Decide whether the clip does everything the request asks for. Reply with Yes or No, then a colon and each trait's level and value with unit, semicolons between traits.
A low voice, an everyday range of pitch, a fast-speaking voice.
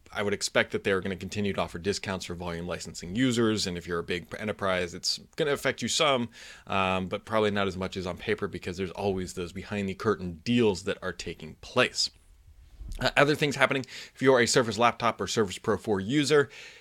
Yes: low, 100 Hz; average, 4.6 semitones; fast, 220 wpm